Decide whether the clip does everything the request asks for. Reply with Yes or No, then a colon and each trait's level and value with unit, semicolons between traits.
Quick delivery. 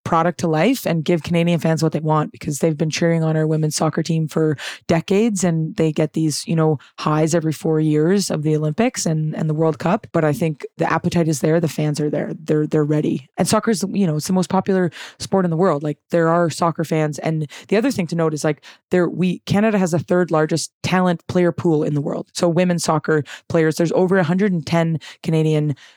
Yes: fast, 230 wpm